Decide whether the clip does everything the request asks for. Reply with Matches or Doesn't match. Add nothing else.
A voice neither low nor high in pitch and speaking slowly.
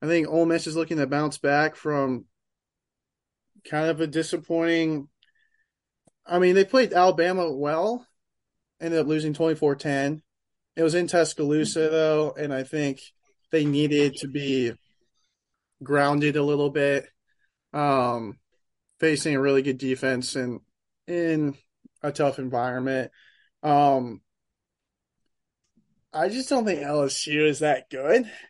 Matches